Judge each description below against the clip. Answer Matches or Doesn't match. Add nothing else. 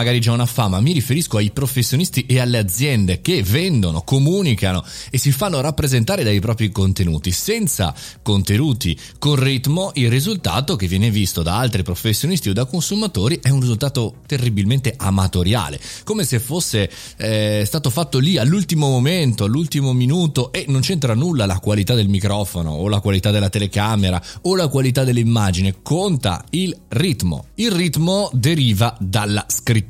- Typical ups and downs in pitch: Doesn't match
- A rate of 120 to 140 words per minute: Doesn't match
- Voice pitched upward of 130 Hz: Doesn't match